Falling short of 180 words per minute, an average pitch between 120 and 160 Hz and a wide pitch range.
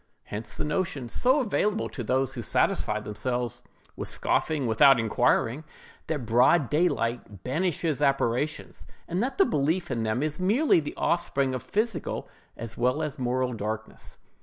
Yes: average, 150 wpm; low, 135 Hz; wide, 5.8 semitones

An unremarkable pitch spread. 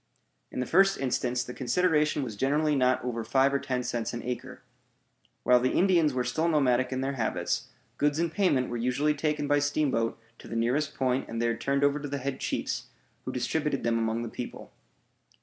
Yes: average, 3.2 semitones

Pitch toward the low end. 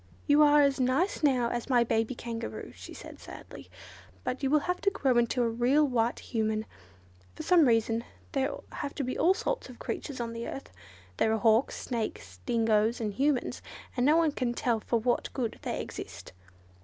No: high, 245 Hz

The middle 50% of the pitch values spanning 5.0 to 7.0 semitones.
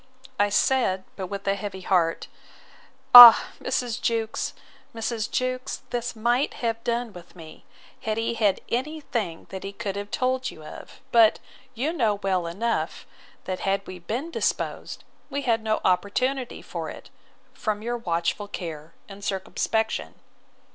No: average, 3.8 semitones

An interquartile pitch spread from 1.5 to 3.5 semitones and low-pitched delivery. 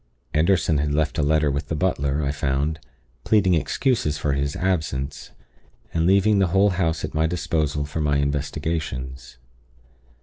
Yes: average, 3.1 semitones; very low, 75 Hz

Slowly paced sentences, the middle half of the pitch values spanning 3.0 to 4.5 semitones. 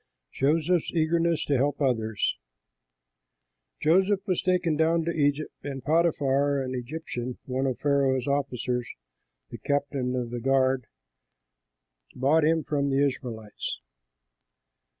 Yes: slow, 115 wpm; average, 3.7 semitones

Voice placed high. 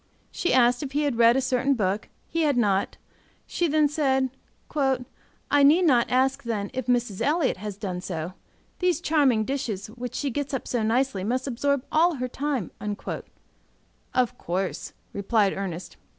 Yes: very high, 250 Hz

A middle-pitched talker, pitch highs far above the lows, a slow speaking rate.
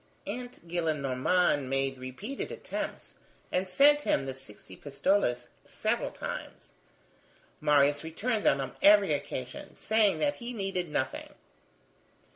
Yes: medium, 160 Hz; wide, 7.2 semitones; slow, 115 wpm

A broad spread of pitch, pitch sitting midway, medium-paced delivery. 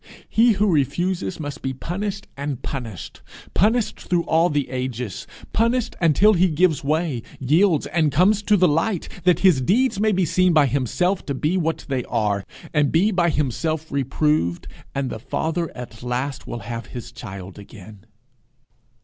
Yes: wide, 6.0 semitones; medium, 155 Hz; average, 160 wpm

